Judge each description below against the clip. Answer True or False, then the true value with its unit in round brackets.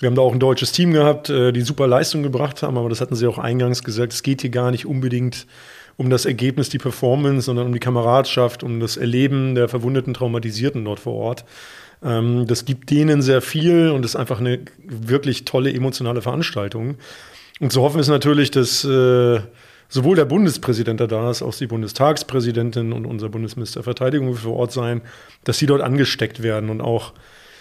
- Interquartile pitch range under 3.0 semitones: True (2.4 semitones)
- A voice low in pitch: True (125 Hz)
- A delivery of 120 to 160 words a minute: False (185 wpm)